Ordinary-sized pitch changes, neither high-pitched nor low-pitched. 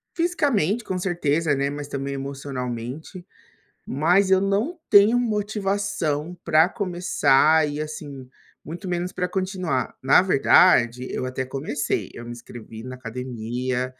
No: wide, 6.4 semitones; medium, 155 Hz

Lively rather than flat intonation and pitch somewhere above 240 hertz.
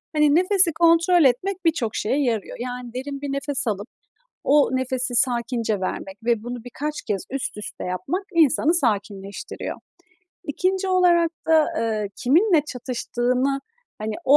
Yes: wide, 5.7 semitones; very high, 260 Hz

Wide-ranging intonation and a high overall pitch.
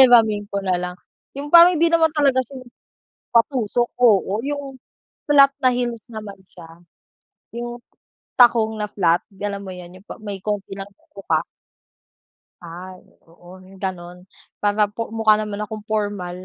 No: average, 4.3 semitones; high, 210 Hz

